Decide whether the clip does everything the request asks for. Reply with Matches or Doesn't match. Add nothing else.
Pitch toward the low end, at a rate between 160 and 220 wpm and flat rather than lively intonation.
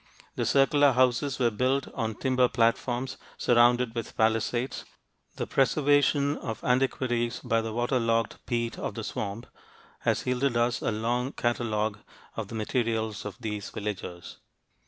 Doesn't match